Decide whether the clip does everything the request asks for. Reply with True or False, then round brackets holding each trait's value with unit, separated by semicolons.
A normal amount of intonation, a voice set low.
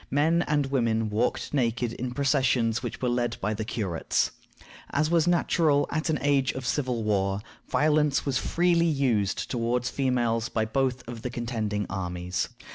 True (4.2 semitones; 125 Hz)